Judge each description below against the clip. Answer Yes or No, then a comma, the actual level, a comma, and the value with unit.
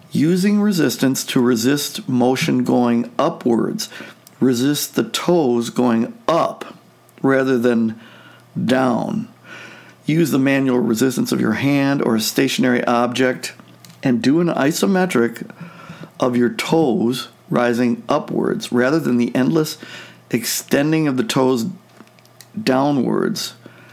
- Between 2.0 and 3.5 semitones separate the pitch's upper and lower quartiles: No, average, 4.6 semitones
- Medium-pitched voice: No, low, 130 Hz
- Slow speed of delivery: Yes, slow, 110 wpm